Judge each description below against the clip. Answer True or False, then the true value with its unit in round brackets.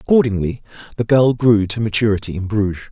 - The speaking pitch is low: True (110 Hz)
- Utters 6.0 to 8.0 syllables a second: True (6.1 syllables/s)